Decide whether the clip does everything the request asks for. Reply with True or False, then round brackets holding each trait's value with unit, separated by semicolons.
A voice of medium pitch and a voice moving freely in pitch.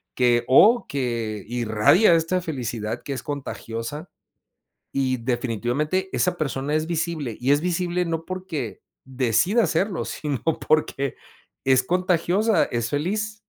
True (145 Hz; 6.3 semitones)